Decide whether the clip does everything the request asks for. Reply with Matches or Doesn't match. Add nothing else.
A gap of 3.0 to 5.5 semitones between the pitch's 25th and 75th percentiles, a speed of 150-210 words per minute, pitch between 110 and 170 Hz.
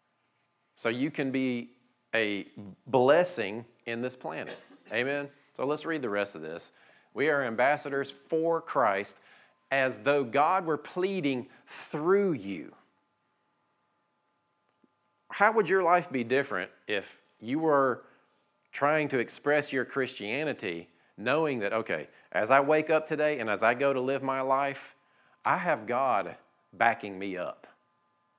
Doesn't match